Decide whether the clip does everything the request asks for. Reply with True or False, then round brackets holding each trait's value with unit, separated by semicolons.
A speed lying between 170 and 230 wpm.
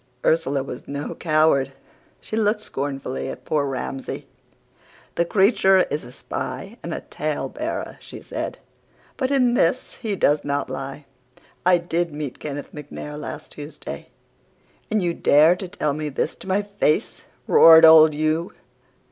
False (150 wpm)